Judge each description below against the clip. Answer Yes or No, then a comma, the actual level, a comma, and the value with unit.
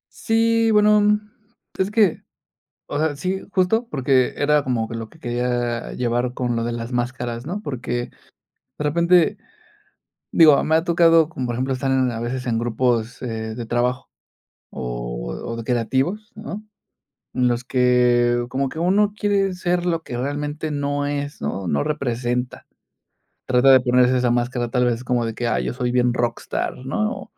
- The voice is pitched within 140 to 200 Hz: No, low, 125 Hz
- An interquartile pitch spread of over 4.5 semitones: Yes, average, 5.0 semitones